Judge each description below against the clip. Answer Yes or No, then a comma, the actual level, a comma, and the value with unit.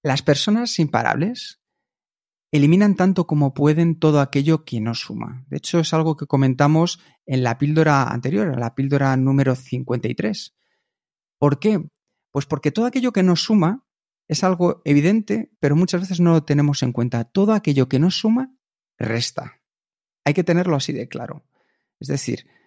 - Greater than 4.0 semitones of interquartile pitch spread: Yes, average, 4.8 semitones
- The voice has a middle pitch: Yes, medium, 155 Hz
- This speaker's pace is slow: No, average, 160 wpm